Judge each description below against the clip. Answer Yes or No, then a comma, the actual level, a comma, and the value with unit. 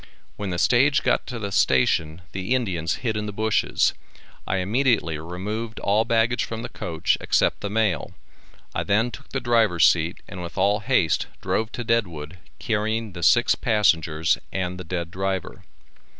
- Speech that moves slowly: No, average, 165 wpm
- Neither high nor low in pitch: No, low, 100 Hz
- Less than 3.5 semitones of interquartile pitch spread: No, average, 4.4 semitones